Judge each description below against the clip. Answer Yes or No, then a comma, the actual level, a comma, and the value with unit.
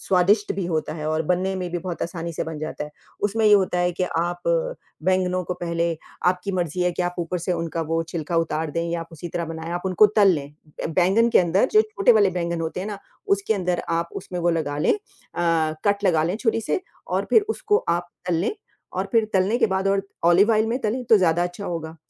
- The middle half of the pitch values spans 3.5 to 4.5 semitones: No, average, 3.0 semitones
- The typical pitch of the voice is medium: Yes, medium, 180 Hz